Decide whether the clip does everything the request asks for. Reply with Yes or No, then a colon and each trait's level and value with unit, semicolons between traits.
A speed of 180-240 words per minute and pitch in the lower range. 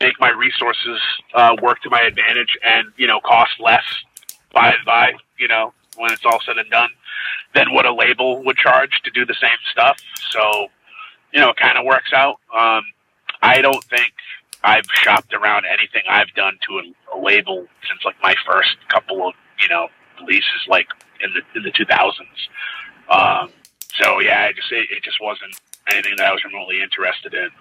Yes: average, 195 wpm; low, 125 Hz